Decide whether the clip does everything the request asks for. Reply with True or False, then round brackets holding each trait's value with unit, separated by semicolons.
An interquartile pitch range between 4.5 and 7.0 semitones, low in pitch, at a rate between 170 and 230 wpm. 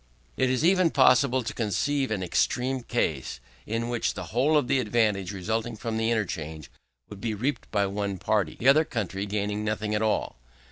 False (3.8 semitones; 110 Hz; 185 wpm)